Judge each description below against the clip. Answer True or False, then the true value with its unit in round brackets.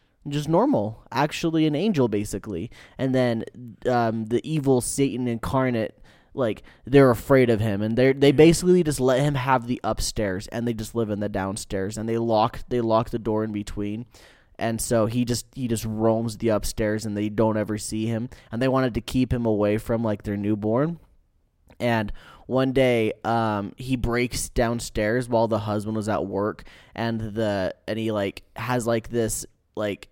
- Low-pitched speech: True (115 Hz)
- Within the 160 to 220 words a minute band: True (185 wpm)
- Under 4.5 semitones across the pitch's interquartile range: True (2.9 semitones)